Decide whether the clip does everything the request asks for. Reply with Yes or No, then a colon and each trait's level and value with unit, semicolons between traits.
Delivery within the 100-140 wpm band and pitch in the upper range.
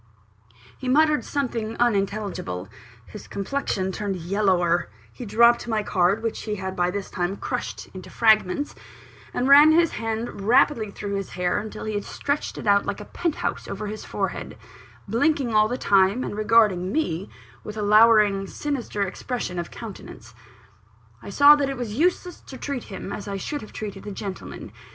No: average, 170 wpm; high, 215 Hz